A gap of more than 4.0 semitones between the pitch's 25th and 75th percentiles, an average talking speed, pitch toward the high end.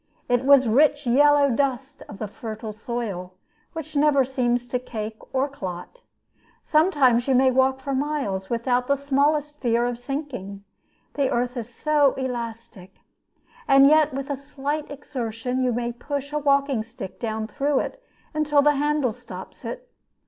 No: average, 3.4 semitones; average, 155 wpm; very high, 260 Hz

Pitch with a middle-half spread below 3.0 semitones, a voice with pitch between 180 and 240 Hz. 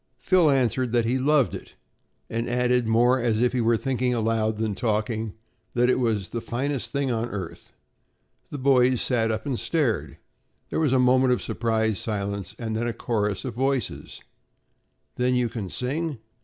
No: narrow, 2.5 semitones; low, 120 Hz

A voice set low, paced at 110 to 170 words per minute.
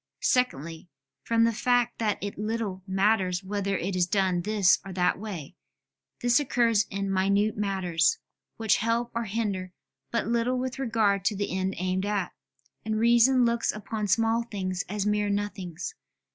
No: high, 205 Hz; average, 160 wpm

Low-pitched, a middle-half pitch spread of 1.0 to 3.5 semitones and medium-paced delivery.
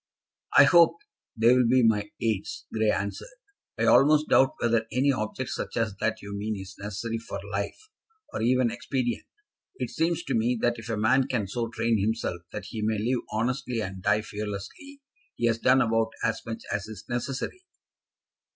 Yes: low, 115 Hz; average, 3.1 semitones; average, 180 wpm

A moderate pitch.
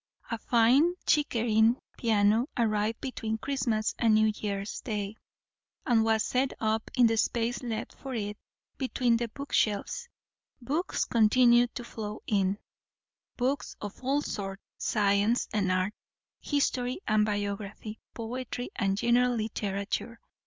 No: high, 225 Hz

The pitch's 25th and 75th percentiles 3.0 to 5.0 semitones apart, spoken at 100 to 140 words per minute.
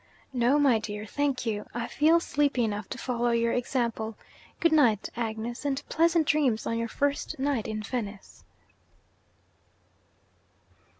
Yes: average, 4.4 semitones; slow, 135 wpm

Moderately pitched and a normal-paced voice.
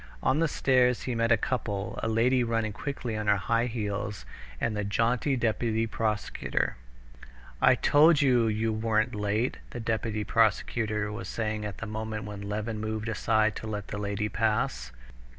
No: low, 110 Hz; average, 165 wpm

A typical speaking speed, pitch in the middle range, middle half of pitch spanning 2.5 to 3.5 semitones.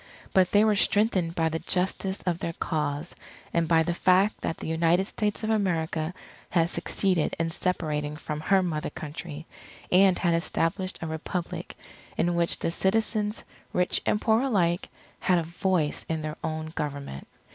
Yes: average, 165 wpm; medium, 170 Hz; average, 2.9 semitones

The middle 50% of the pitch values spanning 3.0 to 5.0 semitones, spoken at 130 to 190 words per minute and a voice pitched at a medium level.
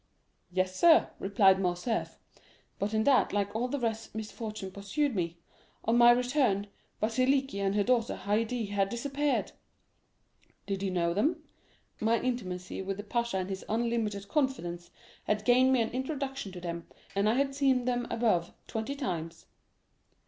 No: average, 4.5 semitones; average, 150 wpm; high, 220 Hz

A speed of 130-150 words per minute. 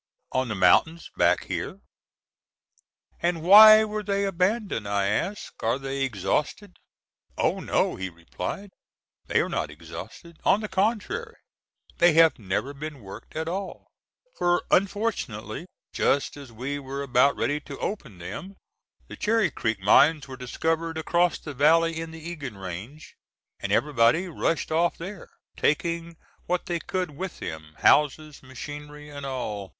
Yes: average, 145 wpm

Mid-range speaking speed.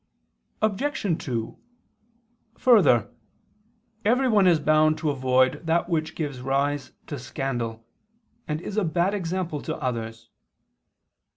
No: slow, 110 wpm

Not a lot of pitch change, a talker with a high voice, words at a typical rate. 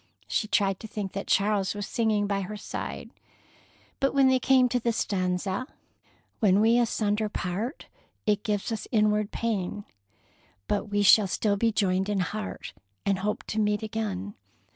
Yes: narrow, 2.0 semitones; high, 210 Hz; average, 165 wpm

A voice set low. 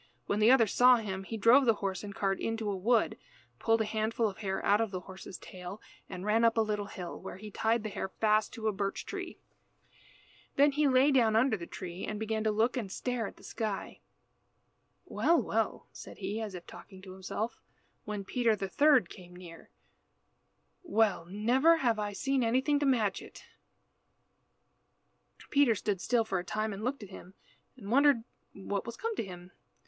No: high, 215 Hz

